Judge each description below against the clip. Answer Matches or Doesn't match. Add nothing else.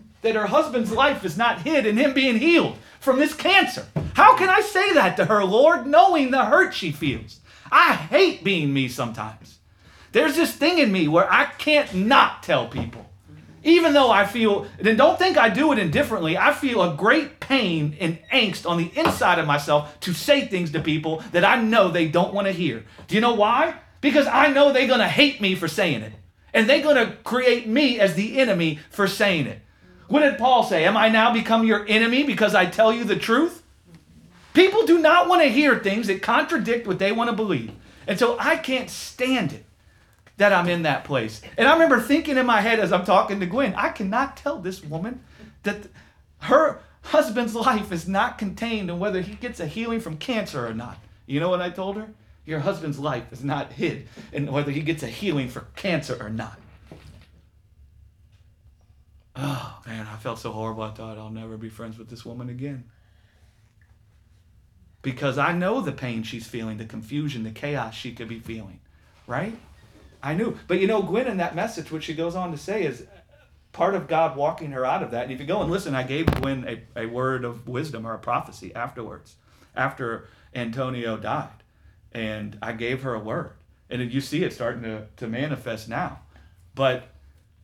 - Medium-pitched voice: Matches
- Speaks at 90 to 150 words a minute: Doesn't match